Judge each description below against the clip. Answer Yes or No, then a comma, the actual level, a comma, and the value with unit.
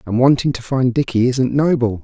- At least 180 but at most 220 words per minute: Yes, fast, 205 wpm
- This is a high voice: No, low, 125 Hz